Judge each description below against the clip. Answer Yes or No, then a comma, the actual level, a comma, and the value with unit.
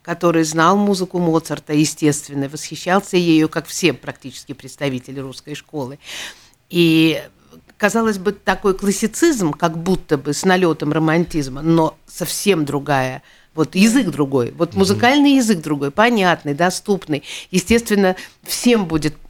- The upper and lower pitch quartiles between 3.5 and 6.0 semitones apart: Yes, average, 4.7 semitones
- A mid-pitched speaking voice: Yes, medium, 165 Hz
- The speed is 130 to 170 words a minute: No, average, 120 wpm